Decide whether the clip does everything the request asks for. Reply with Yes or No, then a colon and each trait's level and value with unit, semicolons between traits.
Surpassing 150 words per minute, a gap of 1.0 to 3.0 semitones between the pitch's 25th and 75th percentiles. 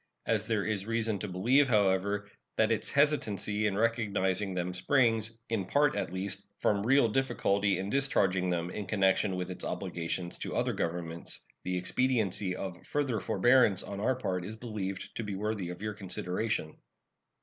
No: average, 165 wpm; average, 3.4 semitones